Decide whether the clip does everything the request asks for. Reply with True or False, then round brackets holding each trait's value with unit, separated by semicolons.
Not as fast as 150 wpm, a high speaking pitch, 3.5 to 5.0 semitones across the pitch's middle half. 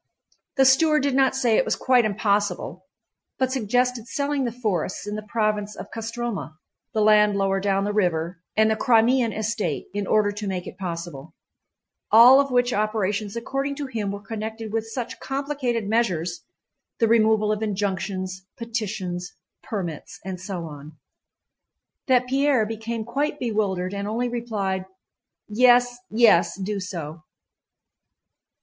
True (140 wpm; 215 Hz; 3.8 semitones)